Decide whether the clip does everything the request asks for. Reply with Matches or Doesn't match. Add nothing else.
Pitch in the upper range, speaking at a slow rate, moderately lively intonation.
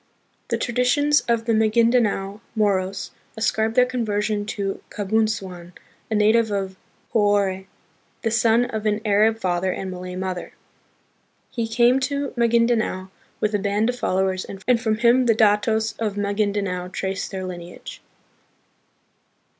Matches